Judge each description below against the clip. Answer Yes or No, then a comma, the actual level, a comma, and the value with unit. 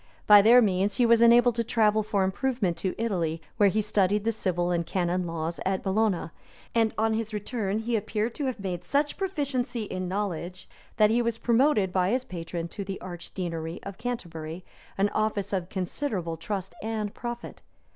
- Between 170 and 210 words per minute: Yes, average, 180 wpm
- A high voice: Yes, high, 205 Hz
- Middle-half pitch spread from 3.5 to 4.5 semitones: Yes, average, 4.0 semitones